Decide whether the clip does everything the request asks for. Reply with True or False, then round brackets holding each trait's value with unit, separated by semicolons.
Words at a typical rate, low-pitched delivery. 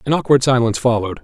True (195 wpm; 125 Hz)